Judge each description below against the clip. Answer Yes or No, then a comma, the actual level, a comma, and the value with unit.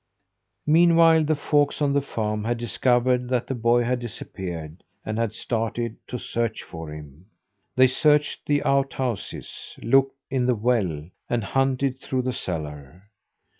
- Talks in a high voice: No, low, 120 Hz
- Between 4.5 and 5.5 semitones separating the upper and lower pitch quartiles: No, average, 4.1 semitones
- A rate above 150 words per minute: No, average, 145 wpm